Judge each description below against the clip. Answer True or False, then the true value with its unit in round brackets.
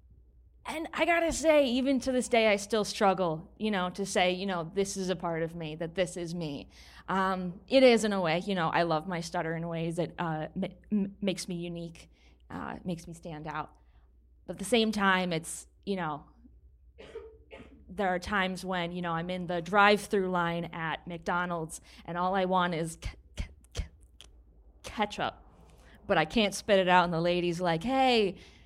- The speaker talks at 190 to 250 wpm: True (200 wpm)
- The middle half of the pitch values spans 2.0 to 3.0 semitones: False (3.4 semitones)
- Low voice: False (180 Hz)